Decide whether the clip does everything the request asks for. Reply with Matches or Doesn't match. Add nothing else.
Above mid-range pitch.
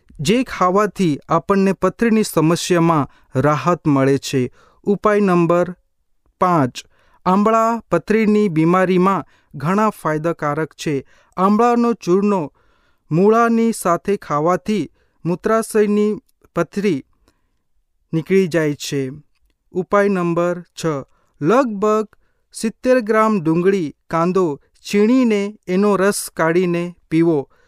Doesn't match